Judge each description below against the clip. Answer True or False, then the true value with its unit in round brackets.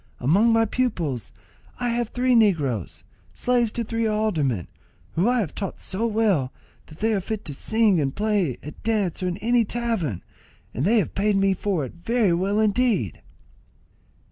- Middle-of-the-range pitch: False (205 Hz)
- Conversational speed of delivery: True (170 wpm)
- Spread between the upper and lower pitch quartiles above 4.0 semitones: True (5.4 semitones)